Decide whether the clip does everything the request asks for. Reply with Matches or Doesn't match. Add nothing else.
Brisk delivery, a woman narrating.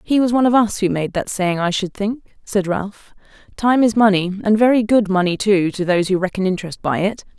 Matches